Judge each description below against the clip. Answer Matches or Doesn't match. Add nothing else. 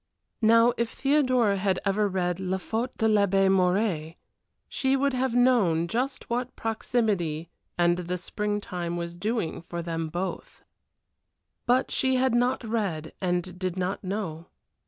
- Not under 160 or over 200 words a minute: Doesn't match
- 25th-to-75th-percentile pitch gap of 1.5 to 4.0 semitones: Doesn't match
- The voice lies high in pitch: Matches